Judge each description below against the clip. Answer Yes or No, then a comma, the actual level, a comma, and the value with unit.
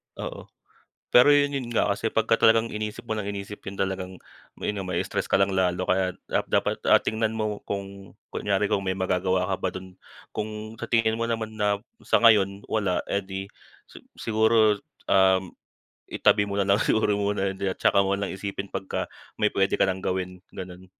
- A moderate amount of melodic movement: No, narrow, 2.3 semitones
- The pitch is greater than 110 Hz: No, low, 100 Hz